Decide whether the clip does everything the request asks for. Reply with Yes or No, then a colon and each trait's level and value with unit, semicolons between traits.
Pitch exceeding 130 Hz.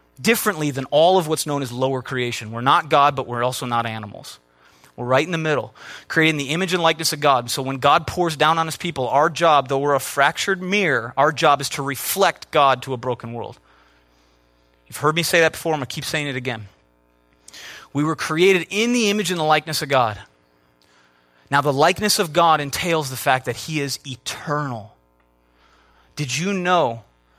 Yes: medium, 140 Hz